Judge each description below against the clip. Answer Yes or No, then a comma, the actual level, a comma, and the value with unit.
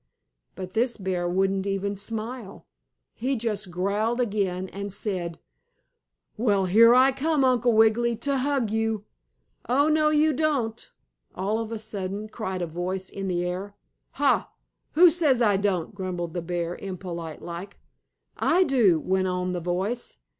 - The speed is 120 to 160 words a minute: Yes, average, 150 wpm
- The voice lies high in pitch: Yes, high, 205 Hz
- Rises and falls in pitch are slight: No, average, 4.4 semitones